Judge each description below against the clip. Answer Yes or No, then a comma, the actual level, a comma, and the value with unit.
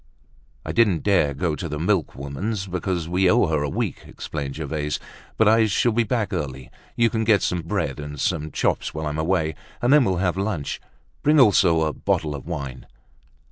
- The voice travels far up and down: Yes, wide, 5.7 semitones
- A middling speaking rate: Yes, average, 190 wpm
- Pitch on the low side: Yes, very low, 85 Hz